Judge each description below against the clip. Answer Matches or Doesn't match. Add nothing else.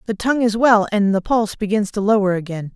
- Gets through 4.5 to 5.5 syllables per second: Doesn't match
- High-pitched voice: Matches